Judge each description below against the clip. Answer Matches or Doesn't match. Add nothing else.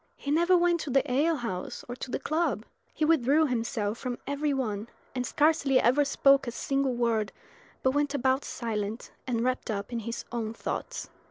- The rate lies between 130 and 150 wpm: Doesn't match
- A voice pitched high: Matches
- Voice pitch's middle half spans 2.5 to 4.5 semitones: Matches